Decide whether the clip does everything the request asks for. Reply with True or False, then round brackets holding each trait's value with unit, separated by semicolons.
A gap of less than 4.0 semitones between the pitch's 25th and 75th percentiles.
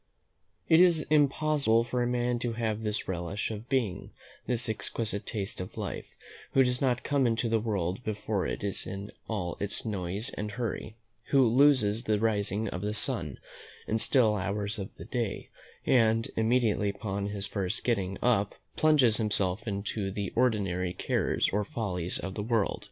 True (3.2 semitones)